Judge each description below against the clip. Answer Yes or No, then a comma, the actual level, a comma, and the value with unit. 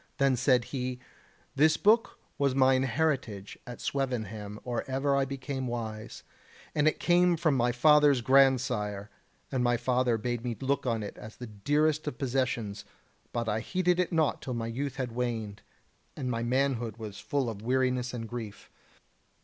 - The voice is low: Yes, low, 125 Hz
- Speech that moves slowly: No, average, 165 wpm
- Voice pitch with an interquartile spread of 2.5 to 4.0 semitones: Yes, average, 3.2 semitones